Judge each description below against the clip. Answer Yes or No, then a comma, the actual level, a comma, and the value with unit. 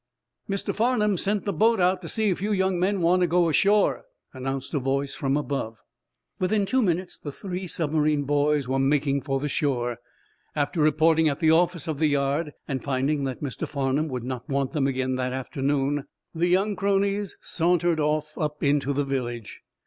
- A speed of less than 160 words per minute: No, average, 185 wpm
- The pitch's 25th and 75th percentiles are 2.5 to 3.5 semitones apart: No, average, 4.6 semitones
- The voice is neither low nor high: Yes, medium, 150 Hz